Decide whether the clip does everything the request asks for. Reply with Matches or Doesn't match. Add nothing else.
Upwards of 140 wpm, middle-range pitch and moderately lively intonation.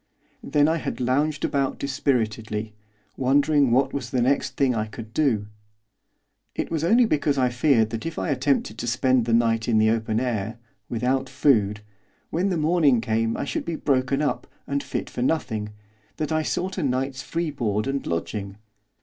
Doesn't match